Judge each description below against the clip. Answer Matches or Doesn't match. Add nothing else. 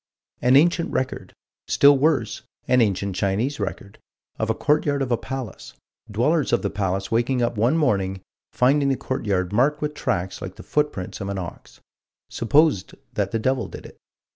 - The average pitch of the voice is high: Doesn't match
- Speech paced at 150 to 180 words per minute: Matches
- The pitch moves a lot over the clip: Matches